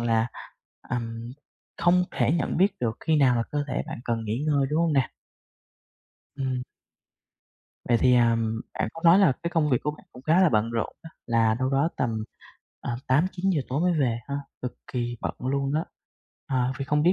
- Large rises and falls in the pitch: No, average, 4.7 semitones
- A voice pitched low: Yes, low, 130 Hz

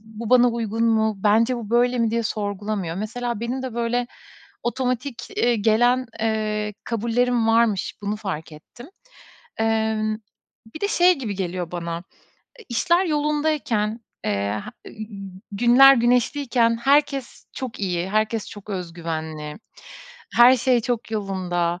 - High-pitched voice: Yes, high, 225 Hz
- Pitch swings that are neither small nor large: Yes, average, 3.3 semitones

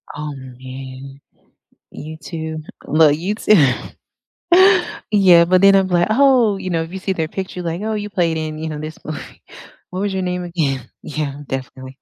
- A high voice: No, medium, 165 Hz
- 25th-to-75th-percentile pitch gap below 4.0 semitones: No, average, 4.5 semitones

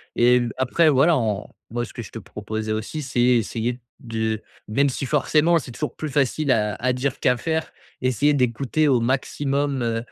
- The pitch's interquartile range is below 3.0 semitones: No, average, 3.7 semitones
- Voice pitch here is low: Yes, low, 125 Hz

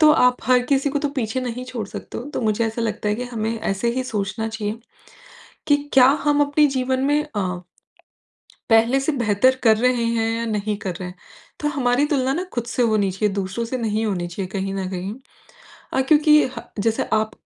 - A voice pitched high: Yes, high, 230 Hz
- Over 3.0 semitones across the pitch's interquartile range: Yes, average, 3.7 semitones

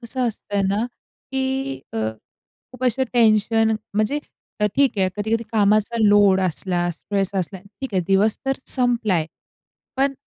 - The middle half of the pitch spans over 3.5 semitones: Yes, average, 3.9 semitones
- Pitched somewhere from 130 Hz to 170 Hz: No, high, 215 Hz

